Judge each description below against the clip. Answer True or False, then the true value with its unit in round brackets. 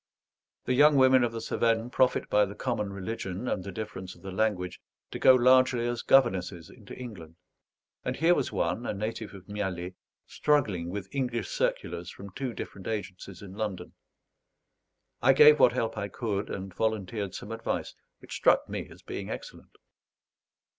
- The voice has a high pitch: False (110 Hz)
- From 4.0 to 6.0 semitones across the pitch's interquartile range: True (4.4 semitones)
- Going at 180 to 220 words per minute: False (165 wpm)